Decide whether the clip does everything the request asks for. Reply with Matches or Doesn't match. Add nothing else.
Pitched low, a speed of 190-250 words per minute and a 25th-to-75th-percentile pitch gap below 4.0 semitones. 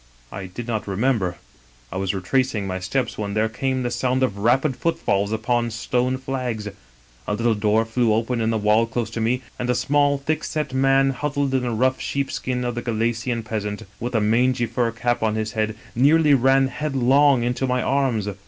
Matches